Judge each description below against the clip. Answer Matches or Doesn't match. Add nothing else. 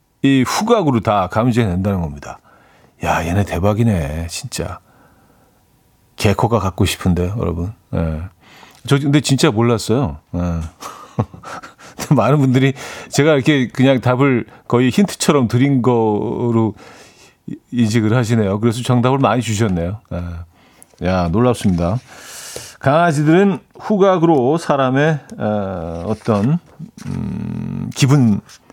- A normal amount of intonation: Doesn't match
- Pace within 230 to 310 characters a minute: Matches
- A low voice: Matches